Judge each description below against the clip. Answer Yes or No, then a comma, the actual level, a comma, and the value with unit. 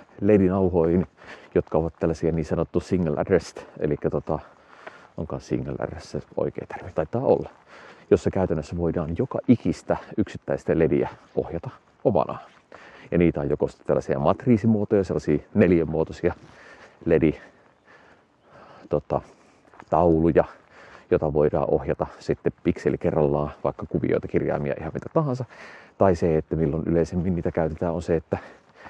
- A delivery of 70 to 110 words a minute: No, average, 120 wpm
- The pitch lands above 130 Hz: No, very low, 85 Hz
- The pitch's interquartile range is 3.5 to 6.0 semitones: No, average, 2.7 semitones